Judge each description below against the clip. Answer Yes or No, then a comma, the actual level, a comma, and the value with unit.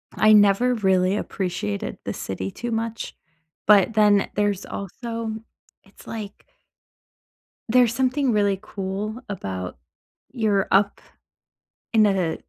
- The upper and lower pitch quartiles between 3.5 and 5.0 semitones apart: No, average, 2.8 semitones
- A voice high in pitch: Yes, high, 205 Hz